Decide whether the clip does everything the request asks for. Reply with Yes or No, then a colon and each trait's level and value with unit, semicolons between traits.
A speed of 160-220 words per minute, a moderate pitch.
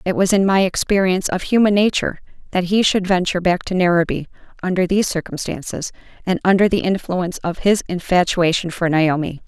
Yes: average, 170 wpm; medium, 180 Hz